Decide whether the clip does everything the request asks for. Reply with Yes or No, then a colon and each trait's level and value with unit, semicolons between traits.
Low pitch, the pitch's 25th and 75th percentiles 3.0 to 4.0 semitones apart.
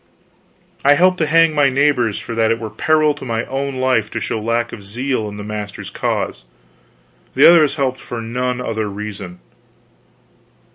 No: low, 120 Hz; average, 4.4 semitones